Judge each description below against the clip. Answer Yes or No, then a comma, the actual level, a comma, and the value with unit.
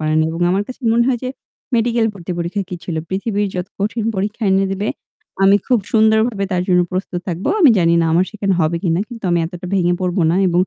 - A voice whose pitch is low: No, high, 195 Hz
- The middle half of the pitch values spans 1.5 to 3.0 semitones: No, average, 3.7 semitones